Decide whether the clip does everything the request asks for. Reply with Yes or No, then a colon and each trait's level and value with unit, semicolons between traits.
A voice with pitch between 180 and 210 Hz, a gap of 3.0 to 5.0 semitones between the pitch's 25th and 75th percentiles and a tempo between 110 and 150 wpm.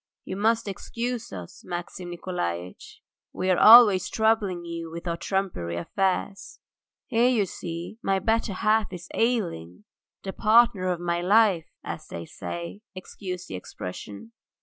Yes: medium, 185 Hz; average, 4.5 semitones; average, 140 wpm